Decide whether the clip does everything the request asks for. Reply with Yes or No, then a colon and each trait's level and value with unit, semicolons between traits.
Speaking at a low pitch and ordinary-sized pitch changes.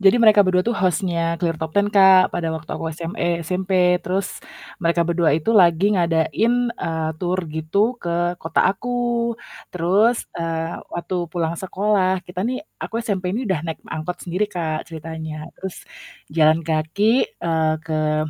No: medium, 175 Hz; average, 3.5 semitones